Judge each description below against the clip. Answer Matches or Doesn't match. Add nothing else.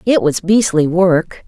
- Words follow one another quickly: Doesn't match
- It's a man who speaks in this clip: Doesn't match